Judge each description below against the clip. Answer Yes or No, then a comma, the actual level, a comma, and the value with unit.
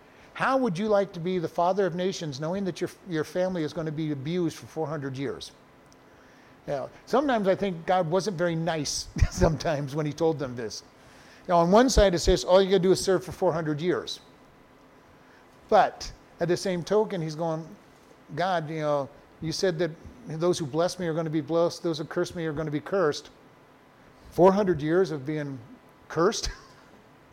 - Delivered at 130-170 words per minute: No, average, 195 wpm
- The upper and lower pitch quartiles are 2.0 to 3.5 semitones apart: Yes, average, 2.8 semitones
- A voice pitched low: No, medium, 170 Hz